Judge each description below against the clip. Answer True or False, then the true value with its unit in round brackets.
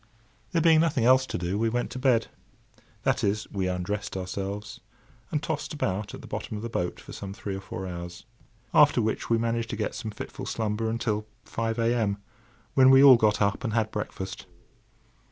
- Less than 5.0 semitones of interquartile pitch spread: True (2.9 semitones)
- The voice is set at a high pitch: False (110 Hz)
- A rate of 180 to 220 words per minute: True (190 wpm)